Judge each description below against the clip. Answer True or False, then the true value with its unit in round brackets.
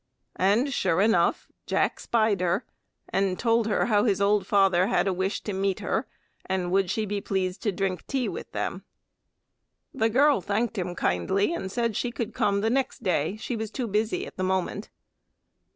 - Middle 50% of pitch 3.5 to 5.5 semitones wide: False (3.1 semitones)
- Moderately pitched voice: False (200 Hz)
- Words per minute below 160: False (185 wpm)